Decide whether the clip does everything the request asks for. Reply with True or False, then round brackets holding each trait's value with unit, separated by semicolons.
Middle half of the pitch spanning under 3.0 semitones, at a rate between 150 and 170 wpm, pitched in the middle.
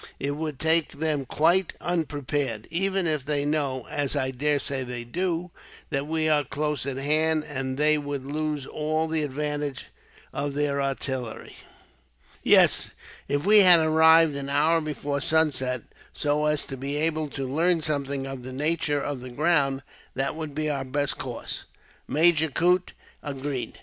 True (2.5 semitones; 160 wpm; 145 Hz)